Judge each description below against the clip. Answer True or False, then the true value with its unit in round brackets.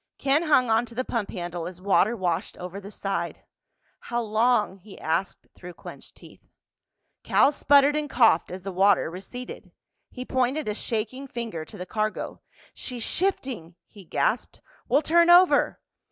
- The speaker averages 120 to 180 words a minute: True (160 wpm)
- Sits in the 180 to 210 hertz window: False (220 Hz)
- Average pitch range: False (5.7 semitones)